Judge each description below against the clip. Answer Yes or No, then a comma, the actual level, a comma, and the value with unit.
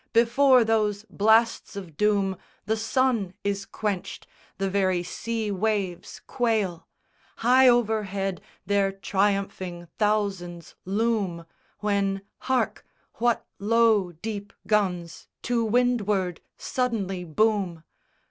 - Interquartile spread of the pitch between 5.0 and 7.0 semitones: No, average, 2.8 semitones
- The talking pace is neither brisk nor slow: No, slow, 100 wpm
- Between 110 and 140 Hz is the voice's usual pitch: No, high, 205 Hz